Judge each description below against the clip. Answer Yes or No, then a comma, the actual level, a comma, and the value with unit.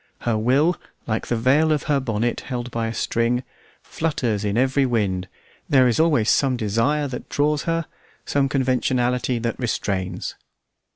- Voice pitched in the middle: No, low, 125 Hz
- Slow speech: No, average, 155 wpm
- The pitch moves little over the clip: No, average, 3.7 semitones